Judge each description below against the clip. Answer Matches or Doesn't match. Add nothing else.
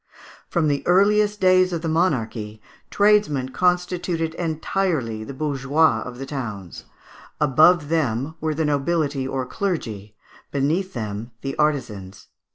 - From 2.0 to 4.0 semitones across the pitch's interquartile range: Doesn't match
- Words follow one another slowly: Matches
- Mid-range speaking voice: Matches